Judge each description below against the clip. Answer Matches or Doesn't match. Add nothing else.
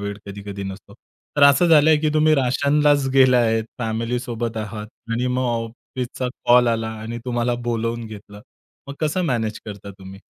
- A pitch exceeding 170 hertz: Doesn't match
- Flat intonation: Doesn't match